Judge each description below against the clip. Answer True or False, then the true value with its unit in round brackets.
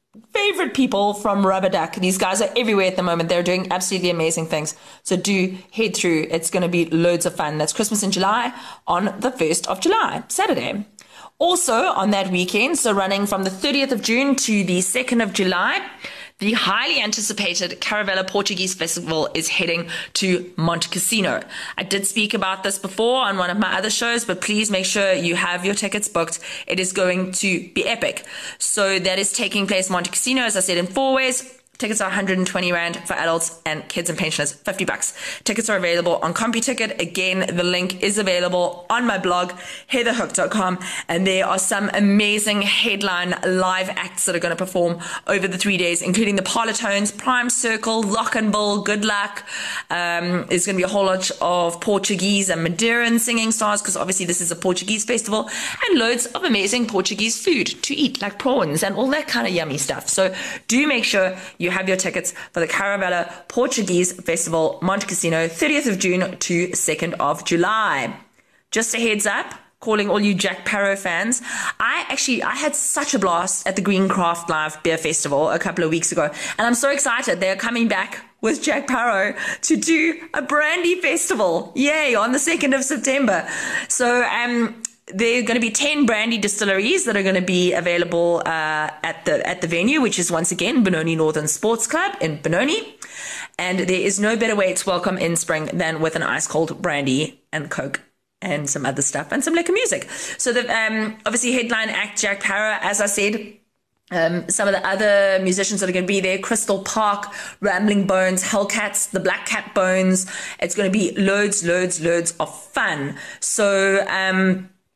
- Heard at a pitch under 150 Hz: False (195 Hz)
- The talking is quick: False (190 wpm)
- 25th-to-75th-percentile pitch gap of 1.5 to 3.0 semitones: False (4.0 semitones)